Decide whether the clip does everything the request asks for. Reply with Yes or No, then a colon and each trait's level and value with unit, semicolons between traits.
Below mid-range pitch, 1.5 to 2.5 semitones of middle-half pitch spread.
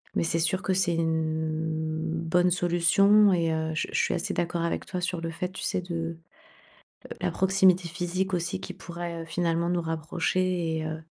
No: medium, 170 Hz; narrow, 1.9 semitones